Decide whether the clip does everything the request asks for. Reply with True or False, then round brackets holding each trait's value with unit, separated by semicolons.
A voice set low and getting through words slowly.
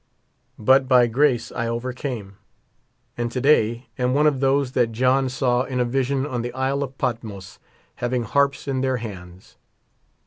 False (125 Hz; 165 wpm)